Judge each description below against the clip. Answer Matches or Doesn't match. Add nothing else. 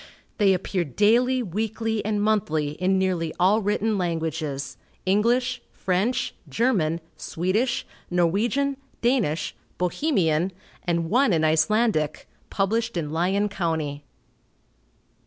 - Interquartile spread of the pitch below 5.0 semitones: Doesn't match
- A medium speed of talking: Doesn't match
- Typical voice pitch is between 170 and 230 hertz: Matches